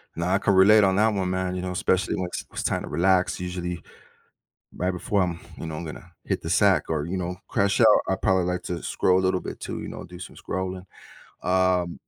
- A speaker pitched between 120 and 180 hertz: No, very low, 90 Hz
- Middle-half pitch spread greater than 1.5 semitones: No, narrow, 1.1 semitones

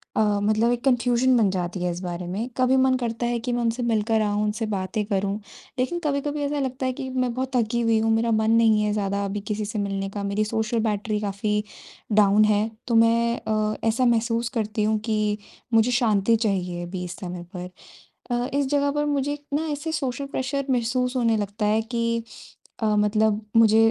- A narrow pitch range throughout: No, average, 3.1 semitones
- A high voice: Yes, high, 225 Hz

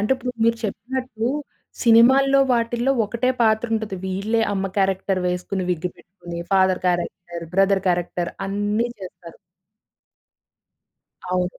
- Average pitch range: Yes, average, 4.1 semitones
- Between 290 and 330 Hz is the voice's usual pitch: No, high, 200 Hz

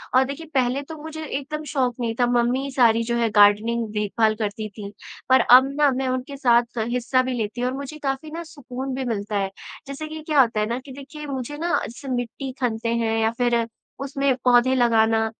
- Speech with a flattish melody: No, average, 3.2 semitones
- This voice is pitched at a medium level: No, very high, 250 Hz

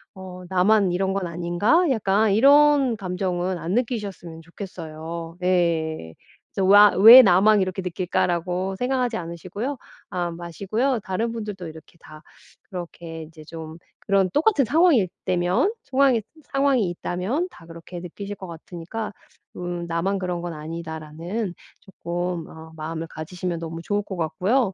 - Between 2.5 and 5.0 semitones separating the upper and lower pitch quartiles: Yes, average, 3.9 semitones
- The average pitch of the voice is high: No, medium, 180 Hz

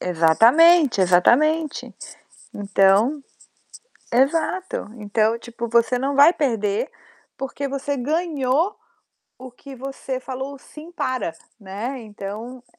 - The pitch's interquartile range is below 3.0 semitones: No, average, 4.7 semitones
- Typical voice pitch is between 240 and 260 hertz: Yes, very high, 255 Hz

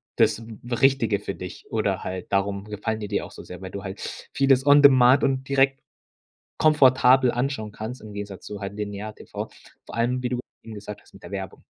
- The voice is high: No, low, 110 Hz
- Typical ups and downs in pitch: Yes, average, 4.5 semitones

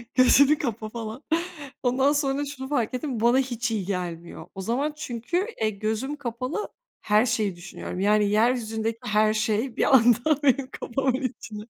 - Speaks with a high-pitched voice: Yes, high, 235 Hz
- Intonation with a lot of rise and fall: No, average, 3.8 semitones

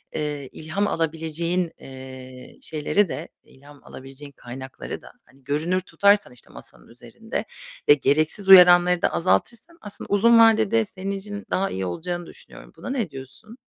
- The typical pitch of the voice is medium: Yes, medium, 165 Hz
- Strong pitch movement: Yes, wide, 6.5 semitones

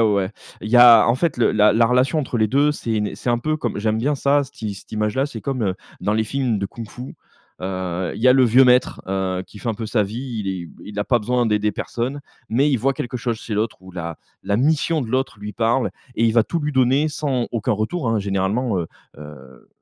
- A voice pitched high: No, low, 115 Hz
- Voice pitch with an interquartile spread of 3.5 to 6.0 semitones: Yes, average, 3.9 semitones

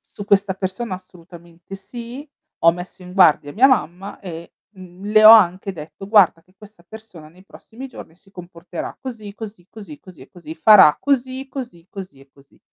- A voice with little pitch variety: No, average, 4.1 semitones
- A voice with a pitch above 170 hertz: Yes, high, 190 Hz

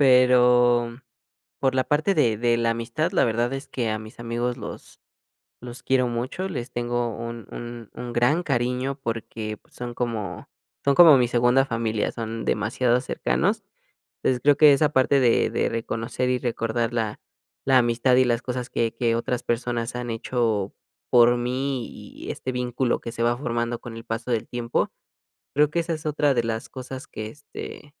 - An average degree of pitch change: No, narrow, 1.9 semitones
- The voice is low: Yes, low, 120 Hz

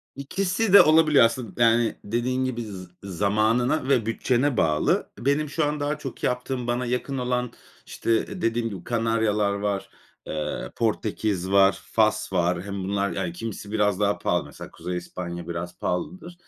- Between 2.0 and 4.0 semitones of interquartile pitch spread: No, average, 4.6 semitones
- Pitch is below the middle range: Yes, low, 115 Hz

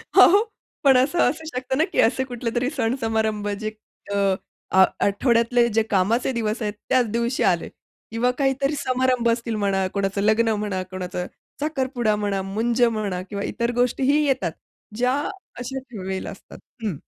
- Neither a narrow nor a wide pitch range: Yes, average, 3.7 semitones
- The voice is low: No, high, 230 Hz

